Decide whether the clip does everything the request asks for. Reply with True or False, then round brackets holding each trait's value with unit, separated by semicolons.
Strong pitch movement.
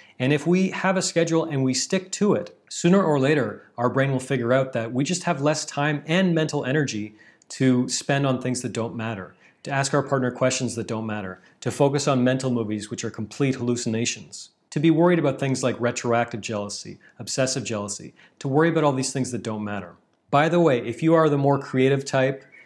False (4.1 semitones)